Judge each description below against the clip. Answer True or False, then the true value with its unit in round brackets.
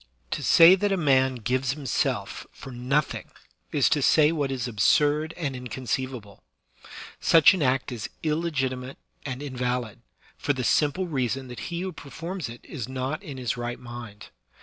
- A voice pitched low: True (130 Hz)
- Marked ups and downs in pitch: False (3.6 semitones)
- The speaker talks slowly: False (170 wpm)